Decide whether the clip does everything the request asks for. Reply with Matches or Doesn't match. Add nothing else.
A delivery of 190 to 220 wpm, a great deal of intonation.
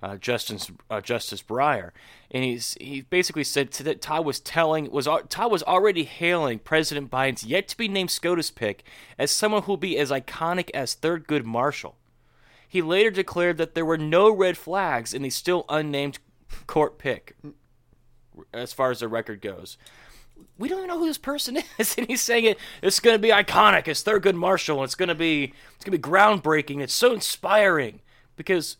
Matches